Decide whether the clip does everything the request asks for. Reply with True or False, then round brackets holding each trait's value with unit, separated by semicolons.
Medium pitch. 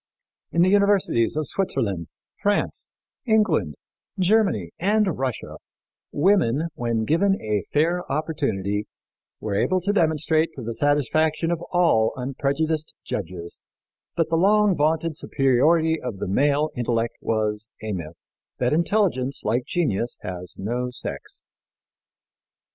True (145 Hz)